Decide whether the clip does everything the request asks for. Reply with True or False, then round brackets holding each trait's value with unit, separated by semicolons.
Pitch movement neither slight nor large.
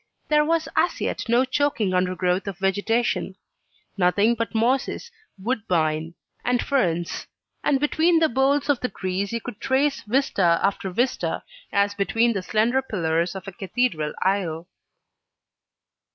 False (6.1 semitones)